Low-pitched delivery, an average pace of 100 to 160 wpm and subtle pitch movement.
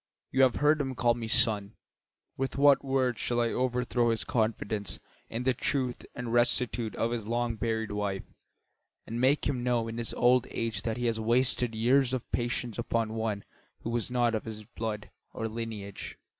No: low, 120 Hz; average, 185 wpm; narrow, 1.9 semitones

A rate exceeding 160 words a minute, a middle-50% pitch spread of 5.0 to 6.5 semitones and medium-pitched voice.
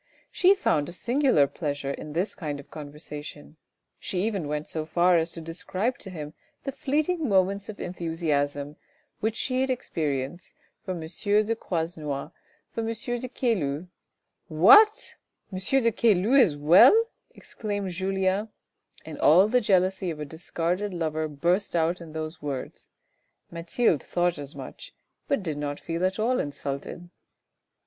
No: average, 155 wpm; wide, 5.6 semitones; medium, 175 Hz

